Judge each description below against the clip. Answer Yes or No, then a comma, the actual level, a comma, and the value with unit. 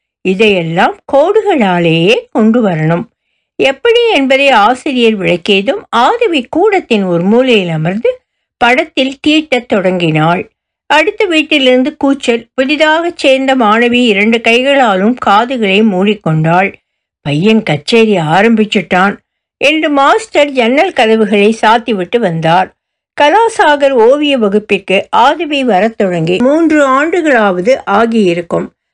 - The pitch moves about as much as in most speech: No, wide, 6.6 semitones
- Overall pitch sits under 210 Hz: No, high, 235 Hz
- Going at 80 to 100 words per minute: Yes, average, 90 wpm